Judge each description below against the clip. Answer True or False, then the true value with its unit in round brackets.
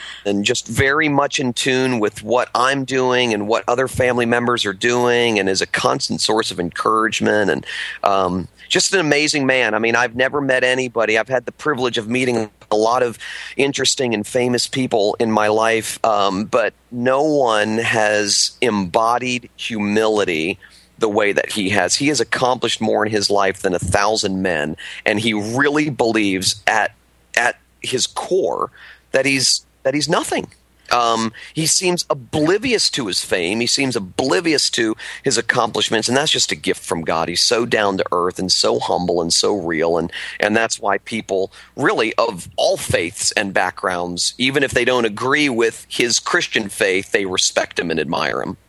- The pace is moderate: True (185 wpm)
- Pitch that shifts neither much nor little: True (3.7 semitones)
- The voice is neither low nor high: False (115 Hz)